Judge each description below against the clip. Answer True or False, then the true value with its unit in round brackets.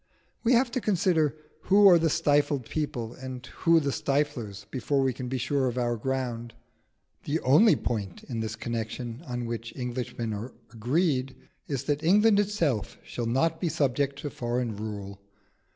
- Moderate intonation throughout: True (4.6 semitones)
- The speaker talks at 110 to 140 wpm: False (165 wpm)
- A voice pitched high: False (130 Hz)